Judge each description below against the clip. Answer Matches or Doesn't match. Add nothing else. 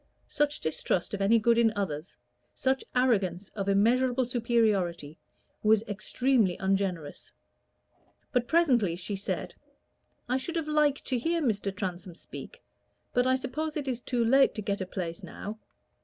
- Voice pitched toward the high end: Matches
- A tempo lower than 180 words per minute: Matches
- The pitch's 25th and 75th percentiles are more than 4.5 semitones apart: Matches